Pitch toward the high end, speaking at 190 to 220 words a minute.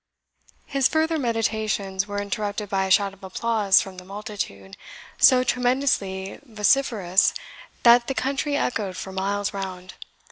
No: high, 205 Hz; slow, 135 wpm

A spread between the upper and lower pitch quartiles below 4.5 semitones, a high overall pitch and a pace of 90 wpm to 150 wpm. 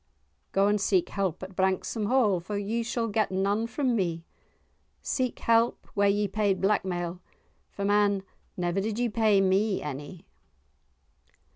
Yes: narrow, 2.5 semitones; high, 200 Hz; average, 140 wpm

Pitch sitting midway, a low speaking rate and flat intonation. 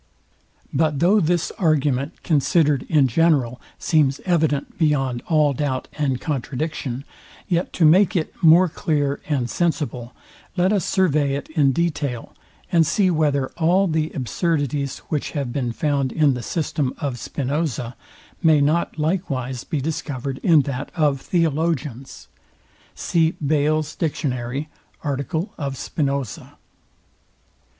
No: medium, 150 Hz; slow, 125 wpm; average, 3.2 semitones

